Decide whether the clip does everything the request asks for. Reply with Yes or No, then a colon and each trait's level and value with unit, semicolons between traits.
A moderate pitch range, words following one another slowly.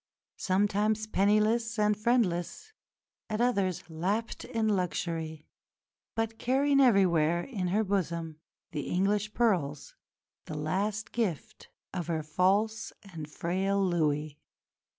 Yes: average, 4.4 semitones; slow, 110 wpm